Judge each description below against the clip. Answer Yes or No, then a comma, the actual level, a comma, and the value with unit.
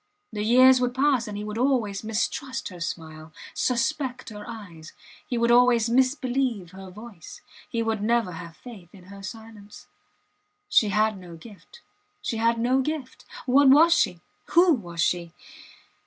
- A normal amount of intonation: Yes, average, 4.4 semitones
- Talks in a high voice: Yes, high, 225 Hz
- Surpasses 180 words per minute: No, average, 155 wpm